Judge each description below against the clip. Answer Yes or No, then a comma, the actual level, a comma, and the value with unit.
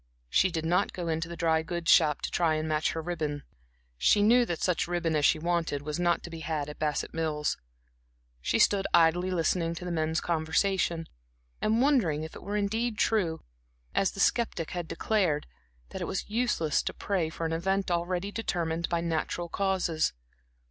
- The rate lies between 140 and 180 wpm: No, average, 190 wpm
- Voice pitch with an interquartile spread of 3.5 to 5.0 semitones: No, average, 2.9 semitones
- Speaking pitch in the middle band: Yes, medium, 170 Hz